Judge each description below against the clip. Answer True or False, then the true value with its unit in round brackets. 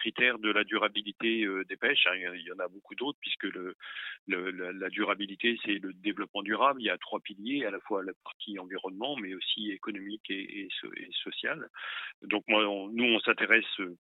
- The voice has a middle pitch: False (110 Hz)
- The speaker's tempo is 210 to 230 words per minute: True (215 wpm)